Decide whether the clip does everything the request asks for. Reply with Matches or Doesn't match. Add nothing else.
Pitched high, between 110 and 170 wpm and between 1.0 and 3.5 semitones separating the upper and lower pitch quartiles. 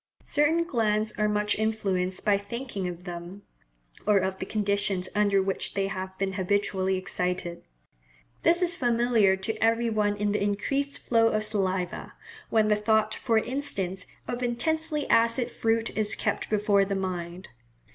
Matches